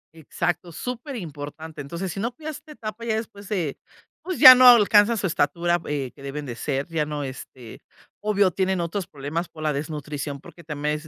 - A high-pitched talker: No, medium, 170 Hz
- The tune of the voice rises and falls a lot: Yes, wide, 6.1 semitones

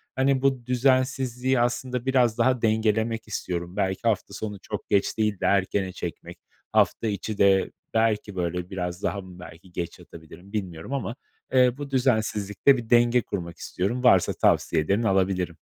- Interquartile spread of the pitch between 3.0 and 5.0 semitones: Yes, average, 4.7 semitones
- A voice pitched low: Yes, low, 110 Hz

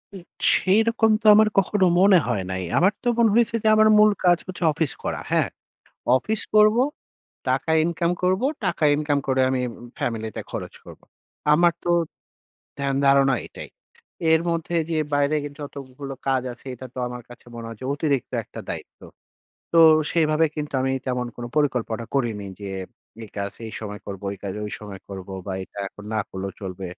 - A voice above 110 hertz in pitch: Yes, medium, 140 Hz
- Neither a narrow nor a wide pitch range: No, wide, 7.3 semitones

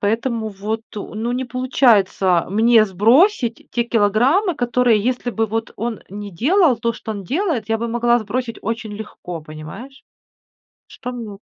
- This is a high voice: Yes, high, 230 Hz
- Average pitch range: Yes, average, 3.1 semitones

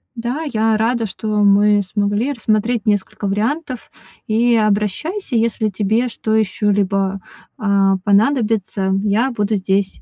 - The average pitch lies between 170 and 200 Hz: No, high, 215 Hz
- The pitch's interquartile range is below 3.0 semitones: Yes, narrow, 2.5 semitones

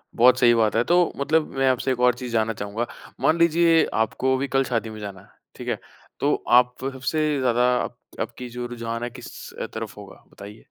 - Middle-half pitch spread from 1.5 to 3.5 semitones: Yes, average, 2.8 semitones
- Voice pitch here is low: Yes, low, 125 Hz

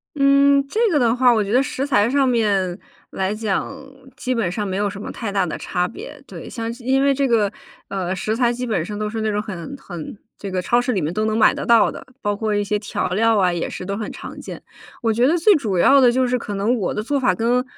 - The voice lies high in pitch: Yes, high, 220 Hz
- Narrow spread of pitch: No, average, 3.9 semitones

